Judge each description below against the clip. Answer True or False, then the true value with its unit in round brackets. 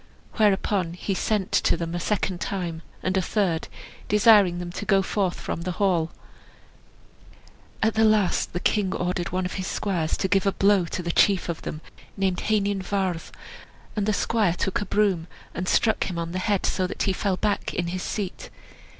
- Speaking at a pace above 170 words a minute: True (195 wpm)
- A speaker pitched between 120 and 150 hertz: False (190 Hz)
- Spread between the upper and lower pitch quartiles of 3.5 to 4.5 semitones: False (2.5 semitones)